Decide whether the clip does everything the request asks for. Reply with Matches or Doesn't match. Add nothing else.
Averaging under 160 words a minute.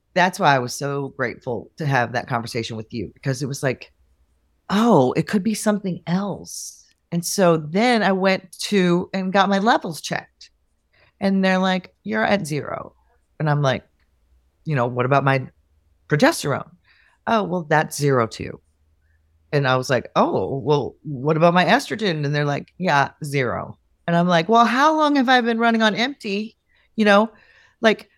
Doesn't match